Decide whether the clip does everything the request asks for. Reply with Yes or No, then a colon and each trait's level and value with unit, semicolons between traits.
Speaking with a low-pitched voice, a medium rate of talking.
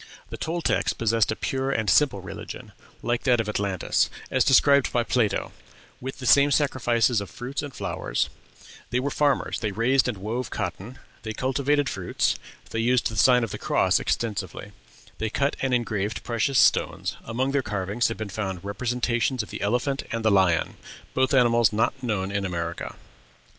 Yes: low, 115 Hz; average, 175 wpm